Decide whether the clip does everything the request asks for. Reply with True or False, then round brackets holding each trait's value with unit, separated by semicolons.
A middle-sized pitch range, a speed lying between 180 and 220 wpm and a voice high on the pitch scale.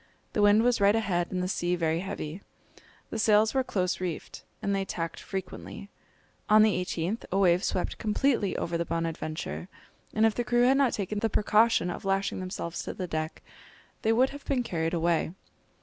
True (4.0 semitones; 190 wpm; 195 Hz)